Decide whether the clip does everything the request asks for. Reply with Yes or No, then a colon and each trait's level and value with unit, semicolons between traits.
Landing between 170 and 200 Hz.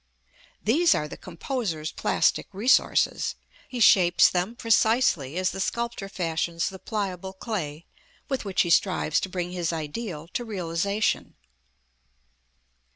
Yes: medium, 185 Hz